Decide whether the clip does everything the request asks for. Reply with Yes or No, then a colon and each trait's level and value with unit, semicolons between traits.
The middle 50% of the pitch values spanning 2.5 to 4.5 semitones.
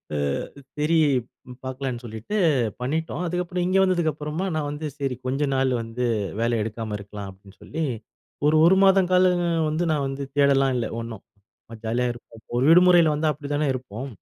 No: average, 5.3 semitones